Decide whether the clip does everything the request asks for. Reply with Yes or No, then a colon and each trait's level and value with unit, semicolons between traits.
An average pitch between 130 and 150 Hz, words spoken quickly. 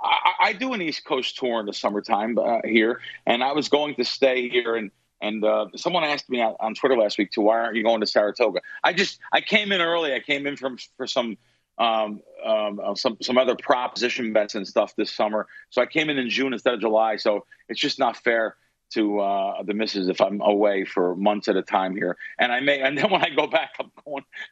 No: low, 115 Hz; fast, 235 wpm